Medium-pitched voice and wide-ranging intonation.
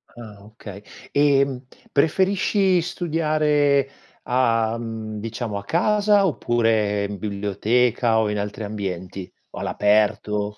No: low, 115 Hz; wide, 5.8 semitones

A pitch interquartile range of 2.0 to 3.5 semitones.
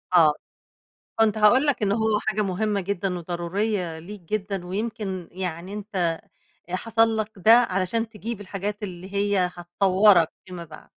Yes: average, 3.1 semitones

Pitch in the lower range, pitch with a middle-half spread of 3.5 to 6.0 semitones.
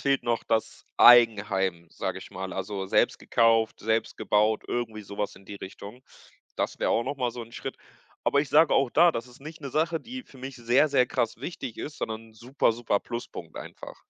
Yes: low, 115 Hz; average, 4.1 semitones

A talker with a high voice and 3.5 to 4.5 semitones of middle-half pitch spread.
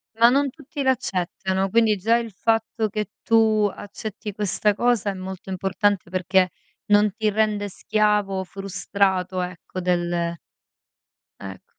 No: high, 205 Hz; average, 2.7 semitones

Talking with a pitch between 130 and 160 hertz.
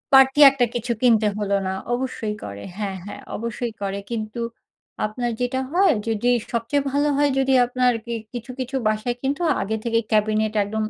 No: high, 235 Hz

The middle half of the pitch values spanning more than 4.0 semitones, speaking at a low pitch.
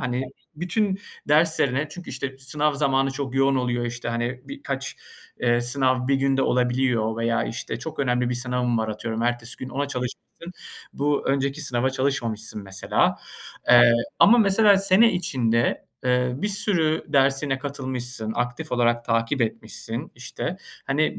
No: average, 3.0 semitones; low, 130 Hz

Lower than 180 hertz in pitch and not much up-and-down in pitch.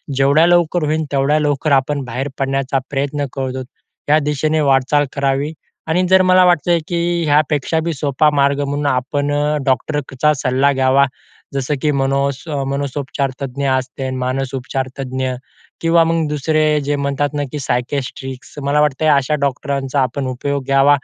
Yes: medium, 140 Hz; narrow, 2.0 semitones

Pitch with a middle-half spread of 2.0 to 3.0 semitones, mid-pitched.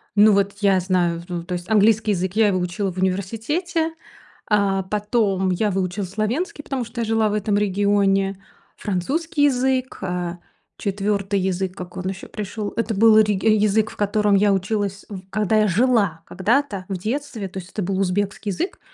No: narrow, 2.5 semitones; high, 205 Hz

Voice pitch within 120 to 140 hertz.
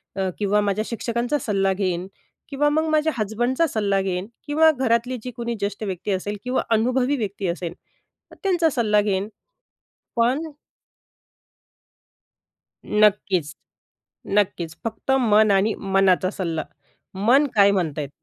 No: high, 210 Hz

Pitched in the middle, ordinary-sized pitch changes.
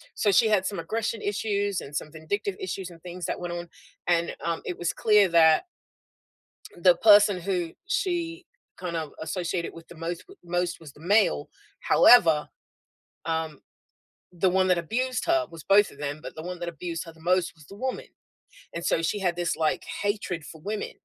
Yes: medium, 175 Hz; average, 3.5 semitones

